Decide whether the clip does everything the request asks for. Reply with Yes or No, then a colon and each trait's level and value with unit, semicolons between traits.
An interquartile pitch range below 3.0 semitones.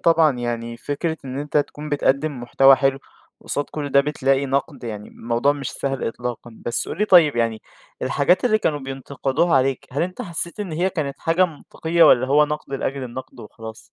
No: average, 3.4 semitones